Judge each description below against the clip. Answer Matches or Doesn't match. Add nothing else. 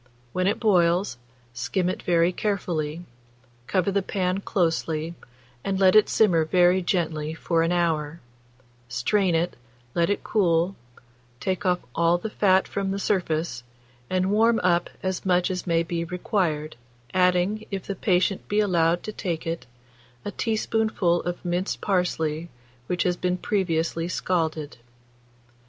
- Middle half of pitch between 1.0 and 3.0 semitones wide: Matches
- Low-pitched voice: Doesn't match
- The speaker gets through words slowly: Doesn't match